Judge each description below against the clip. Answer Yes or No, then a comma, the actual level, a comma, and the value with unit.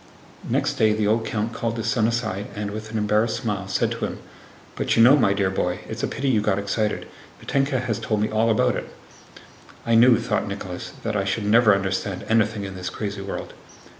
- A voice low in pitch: Yes, low, 110 Hz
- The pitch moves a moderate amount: No, narrow, 2.2 semitones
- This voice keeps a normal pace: No, fast, 215 wpm